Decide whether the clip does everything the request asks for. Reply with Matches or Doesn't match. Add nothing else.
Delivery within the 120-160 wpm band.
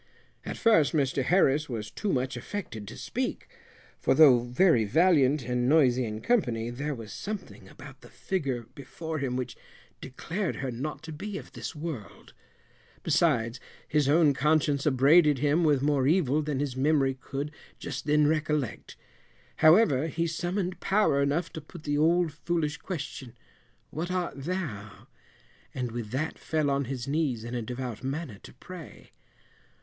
Matches